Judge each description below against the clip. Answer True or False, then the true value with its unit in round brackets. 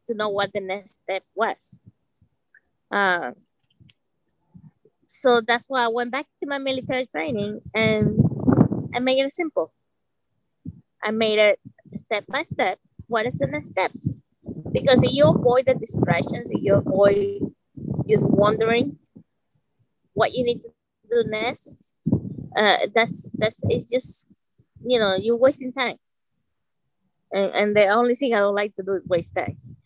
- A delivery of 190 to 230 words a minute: False (150 wpm)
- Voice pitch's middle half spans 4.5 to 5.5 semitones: False (3.7 semitones)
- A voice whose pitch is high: True (225 Hz)